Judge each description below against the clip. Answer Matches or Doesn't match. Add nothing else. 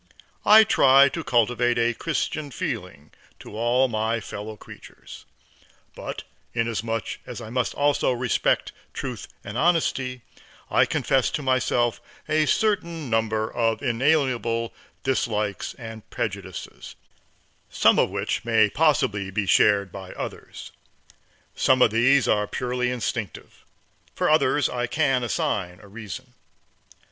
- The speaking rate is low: Matches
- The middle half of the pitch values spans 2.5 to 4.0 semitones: Matches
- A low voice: Matches